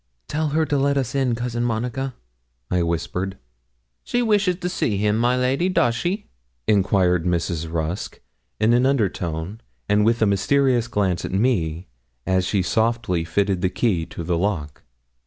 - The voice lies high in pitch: No, low, 110 Hz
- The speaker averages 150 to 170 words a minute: Yes, average, 165 wpm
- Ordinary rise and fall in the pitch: No, wide, 5.9 semitones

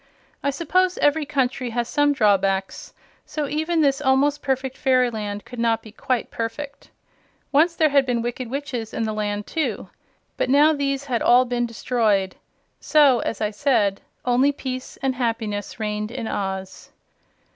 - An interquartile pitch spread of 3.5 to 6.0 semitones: Yes, average, 4.2 semitones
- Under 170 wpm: Yes, average, 155 wpm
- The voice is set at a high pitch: Yes, very high, 250 Hz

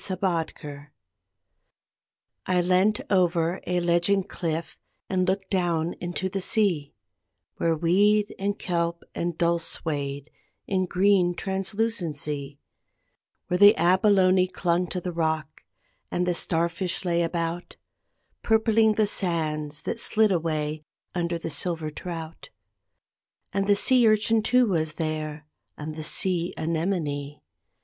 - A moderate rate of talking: No, slow, 125 wpm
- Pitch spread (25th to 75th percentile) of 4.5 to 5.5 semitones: No, average, 3.1 semitones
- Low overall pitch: No, medium, 175 Hz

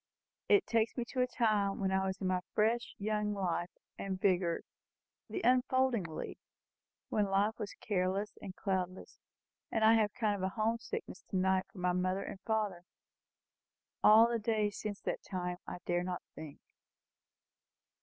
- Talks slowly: No, average, 165 wpm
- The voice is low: No, high, 200 Hz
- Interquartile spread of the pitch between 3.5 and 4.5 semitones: No, average, 3.0 semitones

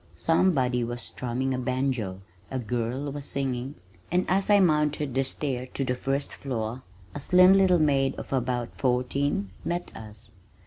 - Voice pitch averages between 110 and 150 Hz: Yes, low, 135 Hz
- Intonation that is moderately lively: Yes, average, 3.1 semitones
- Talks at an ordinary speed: Yes, average, 160 wpm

